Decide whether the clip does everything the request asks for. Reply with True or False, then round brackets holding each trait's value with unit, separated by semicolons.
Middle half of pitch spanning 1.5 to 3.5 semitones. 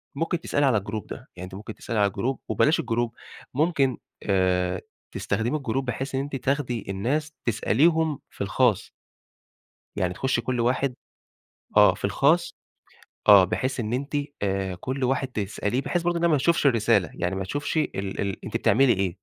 False (5.6 semitones)